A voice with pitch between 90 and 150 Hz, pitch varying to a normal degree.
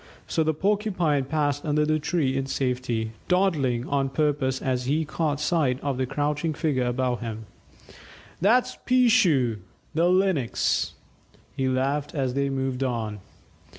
Yes: medium, 140 Hz; average, 3.7 semitones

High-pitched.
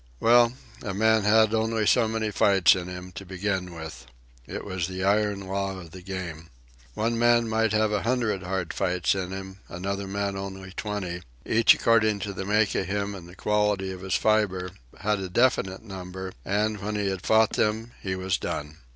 No: low, 100 Hz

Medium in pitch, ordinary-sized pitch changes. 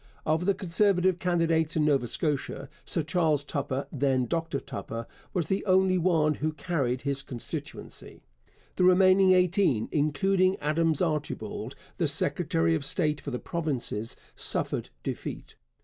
Yes: medium, 160 Hz; average, 4.4 semitones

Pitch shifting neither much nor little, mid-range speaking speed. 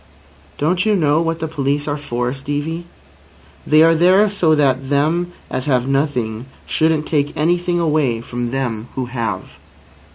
Yes: average, 3.9 semitones; average, 155 wpm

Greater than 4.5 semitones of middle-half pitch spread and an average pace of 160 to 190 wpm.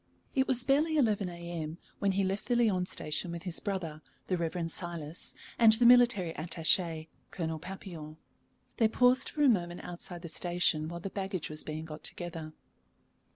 No: average, 4.2 semitones; average, 170 wpm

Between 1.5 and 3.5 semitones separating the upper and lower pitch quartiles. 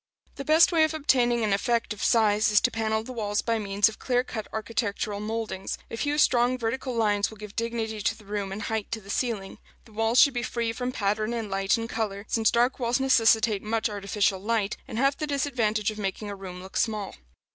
Yes: narrow, 2.6 semitones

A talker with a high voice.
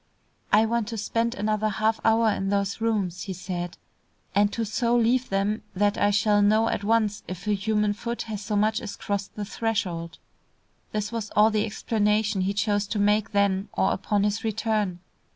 Yes: high, 210 Hz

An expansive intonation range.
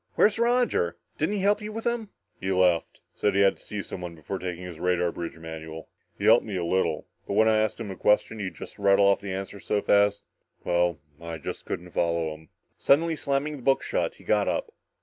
Yes: wide, 7.9 semitones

